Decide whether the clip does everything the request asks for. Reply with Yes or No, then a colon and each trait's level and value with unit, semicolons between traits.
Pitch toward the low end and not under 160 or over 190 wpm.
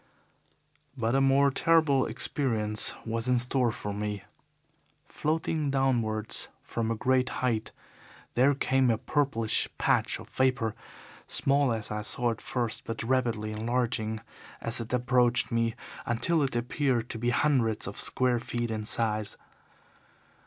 No: low, 120 Hz; average, 140 wpm